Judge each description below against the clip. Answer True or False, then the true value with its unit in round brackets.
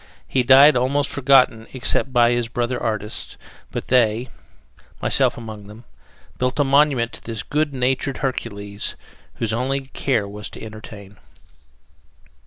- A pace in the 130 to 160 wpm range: True (135 wpm)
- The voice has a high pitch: False (120 Hz)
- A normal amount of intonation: True (3.3 semitones)